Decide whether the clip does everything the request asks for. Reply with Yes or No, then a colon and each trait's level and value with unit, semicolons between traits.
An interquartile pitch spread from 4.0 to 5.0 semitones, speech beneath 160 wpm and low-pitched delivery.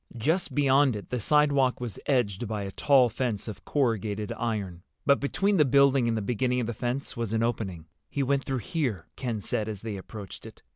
No: average, 4.4 semitones; fast, 205 wpm; low, 120 Hz